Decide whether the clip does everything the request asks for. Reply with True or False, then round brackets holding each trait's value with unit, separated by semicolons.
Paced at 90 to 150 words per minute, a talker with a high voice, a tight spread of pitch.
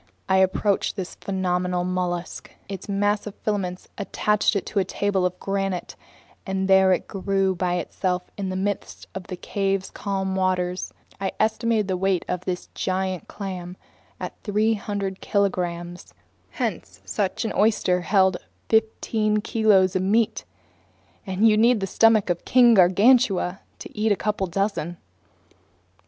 True (145 wpm; 195 Hz; 2.1 semitones)